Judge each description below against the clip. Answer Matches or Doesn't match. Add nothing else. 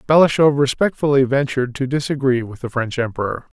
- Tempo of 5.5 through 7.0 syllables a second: Matches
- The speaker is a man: Matches